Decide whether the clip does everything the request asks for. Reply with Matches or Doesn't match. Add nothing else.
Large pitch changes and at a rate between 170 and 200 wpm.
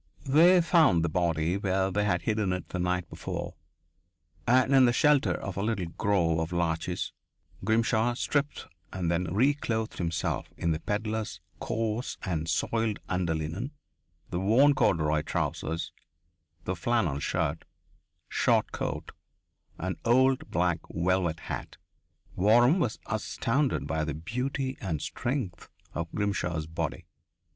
Doesn't match